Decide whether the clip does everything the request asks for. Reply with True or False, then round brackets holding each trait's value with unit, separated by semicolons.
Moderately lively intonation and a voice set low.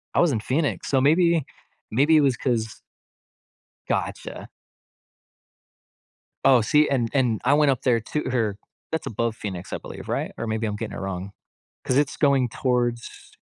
True (4.2 semitones; 125 Hz)